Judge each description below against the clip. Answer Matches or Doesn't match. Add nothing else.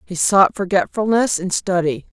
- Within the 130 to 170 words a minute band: Matches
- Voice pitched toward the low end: Doesn't match